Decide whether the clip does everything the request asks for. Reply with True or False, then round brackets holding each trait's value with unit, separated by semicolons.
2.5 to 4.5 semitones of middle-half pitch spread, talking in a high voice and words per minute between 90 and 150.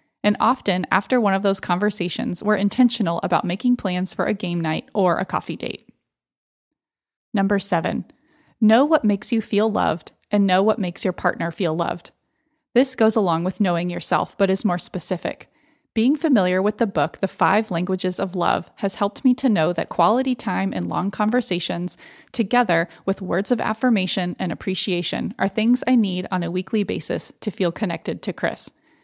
False (4.0 semitones; 195 Hz; 180 wpm)